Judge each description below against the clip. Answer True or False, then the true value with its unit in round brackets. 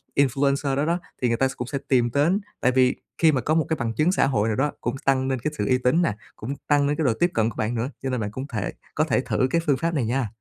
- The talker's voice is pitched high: False (135 Hz)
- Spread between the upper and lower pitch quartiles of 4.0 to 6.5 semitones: False (3.5 semitones)